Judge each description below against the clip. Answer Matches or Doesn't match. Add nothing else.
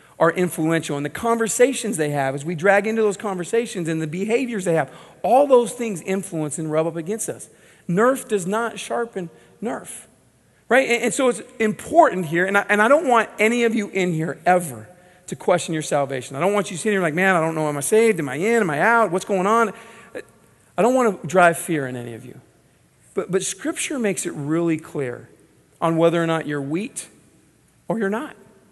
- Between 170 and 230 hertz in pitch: Matches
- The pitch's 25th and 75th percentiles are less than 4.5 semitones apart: Doesn't match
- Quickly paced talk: Matches